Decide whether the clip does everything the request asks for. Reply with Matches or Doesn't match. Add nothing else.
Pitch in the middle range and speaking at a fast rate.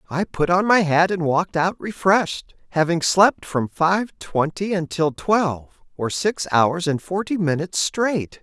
Doesn't match